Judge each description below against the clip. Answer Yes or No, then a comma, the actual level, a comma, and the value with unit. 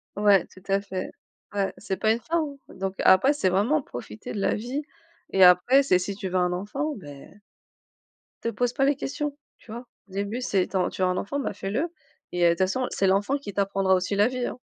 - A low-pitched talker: No, high, 200 Hz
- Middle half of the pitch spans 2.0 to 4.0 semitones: No, average, 5.2 semitones